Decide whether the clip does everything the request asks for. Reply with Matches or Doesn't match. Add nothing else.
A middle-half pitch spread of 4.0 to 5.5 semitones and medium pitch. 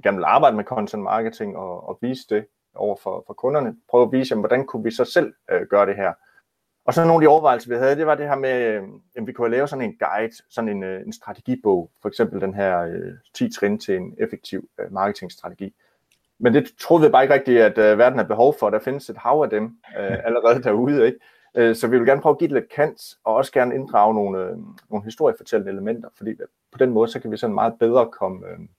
Doesn't match